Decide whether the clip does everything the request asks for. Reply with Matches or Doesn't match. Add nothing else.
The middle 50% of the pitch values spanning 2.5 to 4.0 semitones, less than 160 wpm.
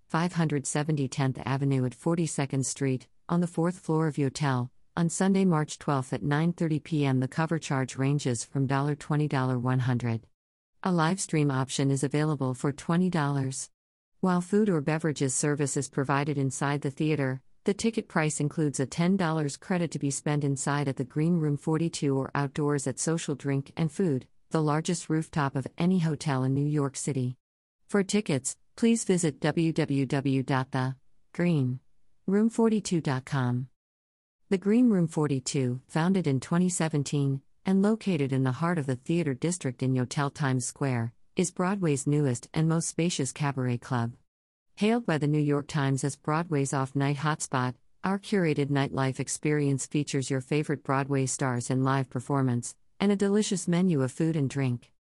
Matches